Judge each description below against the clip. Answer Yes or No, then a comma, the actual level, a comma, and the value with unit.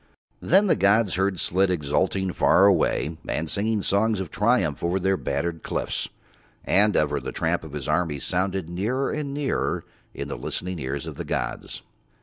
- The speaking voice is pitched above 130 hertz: No, very low, 95 Hz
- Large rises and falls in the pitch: No, average, 4.0 semitones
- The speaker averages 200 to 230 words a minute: No, average, 170 wpm